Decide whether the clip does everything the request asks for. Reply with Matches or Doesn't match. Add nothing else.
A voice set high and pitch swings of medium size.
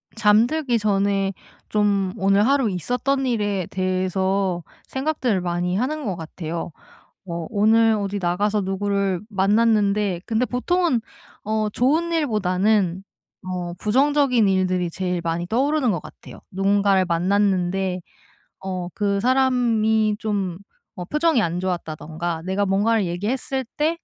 Matches